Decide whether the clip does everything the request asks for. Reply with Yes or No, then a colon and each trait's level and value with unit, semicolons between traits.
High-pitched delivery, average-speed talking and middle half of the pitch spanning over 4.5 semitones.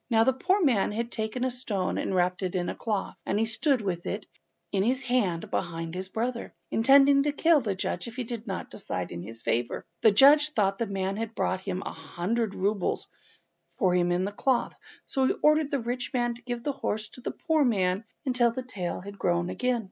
No: high, 225 Hz; fast, 220 wpm; average, 5.1 semitones